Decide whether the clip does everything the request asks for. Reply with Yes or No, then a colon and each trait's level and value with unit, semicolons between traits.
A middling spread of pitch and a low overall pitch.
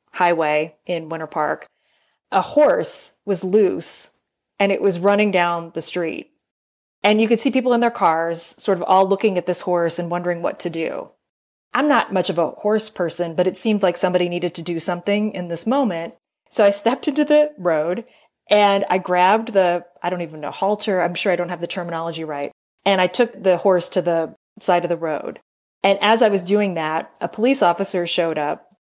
No: average, 3.2 semitones; medium, 180 Hz